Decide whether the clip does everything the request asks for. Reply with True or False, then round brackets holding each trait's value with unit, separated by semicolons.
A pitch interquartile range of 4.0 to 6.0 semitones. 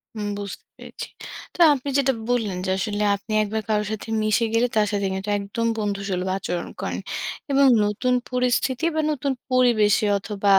False (3.4 semitones)